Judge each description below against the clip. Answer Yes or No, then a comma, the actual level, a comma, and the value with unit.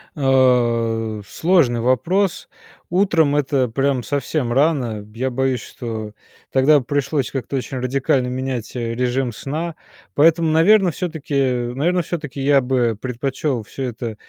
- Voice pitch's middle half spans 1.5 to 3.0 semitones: No, average, 3.5 semitones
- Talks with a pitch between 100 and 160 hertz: Yes, low, 135 Hz